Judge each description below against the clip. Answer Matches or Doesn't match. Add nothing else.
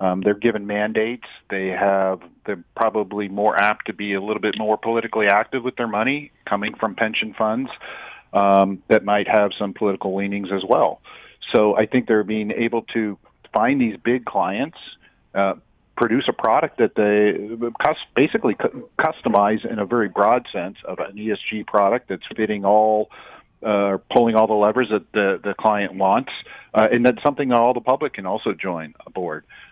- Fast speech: Doesn't match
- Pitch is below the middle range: Matches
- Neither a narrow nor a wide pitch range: Doesn't match